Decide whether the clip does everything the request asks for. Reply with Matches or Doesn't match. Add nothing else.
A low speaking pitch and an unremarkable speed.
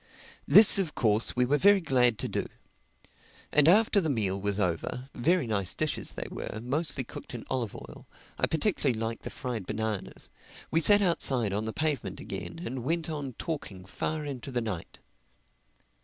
Matches